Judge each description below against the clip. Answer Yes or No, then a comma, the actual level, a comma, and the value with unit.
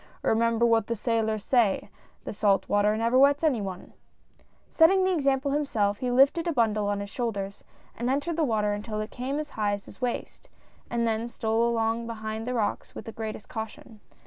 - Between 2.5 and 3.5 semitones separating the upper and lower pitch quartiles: Yes, average, 3.2 semitones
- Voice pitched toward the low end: No, high, 230 Hz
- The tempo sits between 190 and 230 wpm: Yes, average, 200 wpm